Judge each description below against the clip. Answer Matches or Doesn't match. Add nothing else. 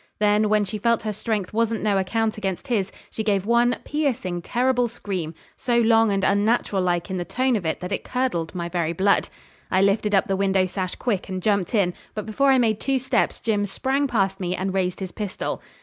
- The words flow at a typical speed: Doesn't match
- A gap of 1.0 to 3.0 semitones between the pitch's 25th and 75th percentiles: Doesn't match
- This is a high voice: Matches